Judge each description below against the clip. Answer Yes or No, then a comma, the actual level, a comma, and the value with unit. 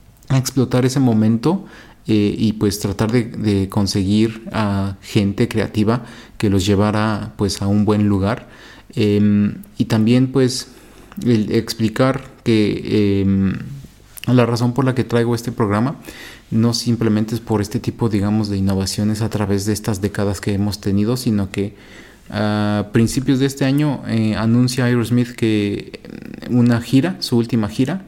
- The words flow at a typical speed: Yes, average, 150 wpm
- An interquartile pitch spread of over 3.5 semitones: No, average, 2.9 semitones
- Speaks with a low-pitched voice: Yes, low, 110 Hz